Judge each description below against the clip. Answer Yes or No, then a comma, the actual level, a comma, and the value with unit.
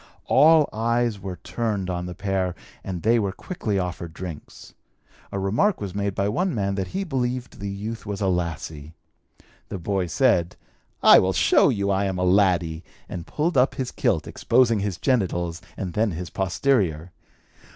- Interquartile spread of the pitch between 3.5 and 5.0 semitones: Yes, average, 4.3 semitones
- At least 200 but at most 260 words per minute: No, average, 170 wpm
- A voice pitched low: Yes, low, 100 Hz